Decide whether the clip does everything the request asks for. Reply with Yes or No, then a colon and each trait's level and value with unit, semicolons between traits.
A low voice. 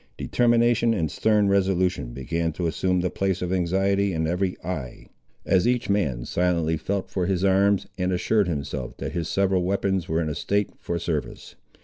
Yes: very low, 90 Hz